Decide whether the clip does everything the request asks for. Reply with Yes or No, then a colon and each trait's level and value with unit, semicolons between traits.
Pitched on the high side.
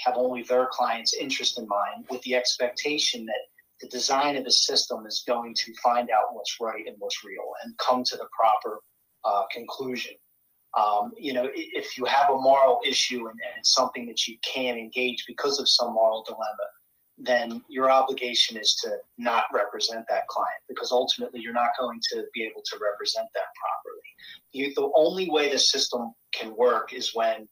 No: low, 125 Hz